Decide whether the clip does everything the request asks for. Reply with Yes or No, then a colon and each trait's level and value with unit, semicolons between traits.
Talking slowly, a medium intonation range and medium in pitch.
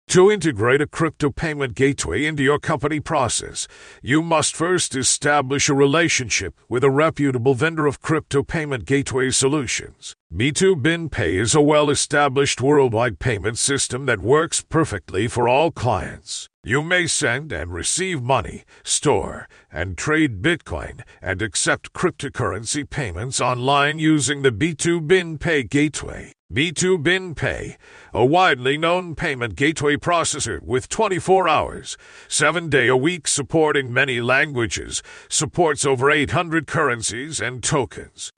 Yes: slow, 125 wpm; average, 3.4 semitones; medium, 145 Hz